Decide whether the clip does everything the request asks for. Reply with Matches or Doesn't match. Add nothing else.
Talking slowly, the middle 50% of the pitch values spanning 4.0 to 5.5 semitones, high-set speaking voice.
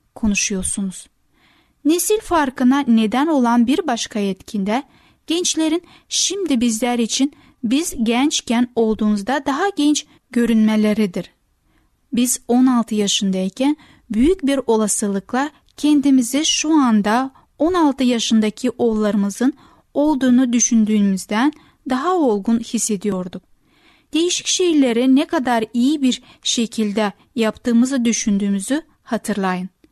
Matches